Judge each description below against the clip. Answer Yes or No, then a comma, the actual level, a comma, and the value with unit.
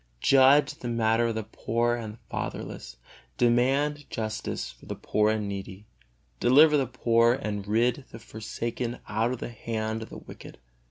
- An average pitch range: No, narrow, 2.3 semitones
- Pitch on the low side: Yes, low, 115 Hz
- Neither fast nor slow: Yes, average, 160 wpm